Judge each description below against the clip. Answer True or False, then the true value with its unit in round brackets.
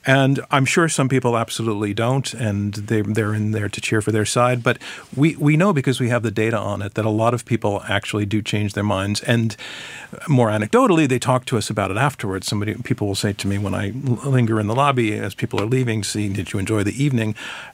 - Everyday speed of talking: False (235 wpm)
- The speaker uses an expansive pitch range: False (3.7 semitones)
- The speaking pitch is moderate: False (110 Hz)